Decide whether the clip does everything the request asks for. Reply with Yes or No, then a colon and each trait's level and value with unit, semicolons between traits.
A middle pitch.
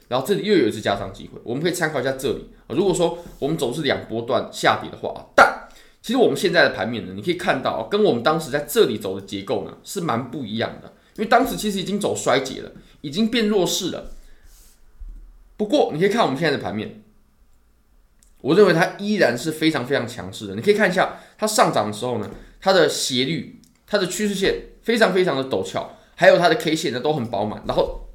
Yes: medium, 165 Hz